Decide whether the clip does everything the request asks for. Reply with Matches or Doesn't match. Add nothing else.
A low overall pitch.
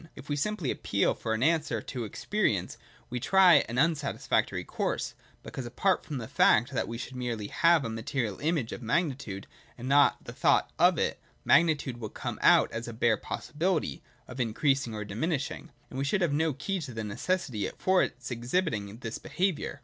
Matches